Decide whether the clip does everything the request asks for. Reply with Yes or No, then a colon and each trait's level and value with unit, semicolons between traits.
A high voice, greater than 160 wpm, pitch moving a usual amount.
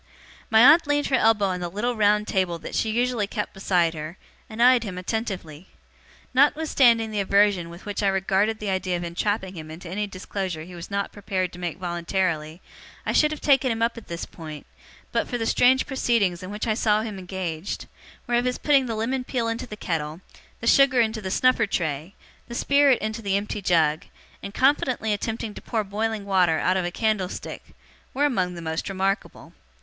Yes: high, 205 Hz; average, 200 wpm; average, 4.3 semitones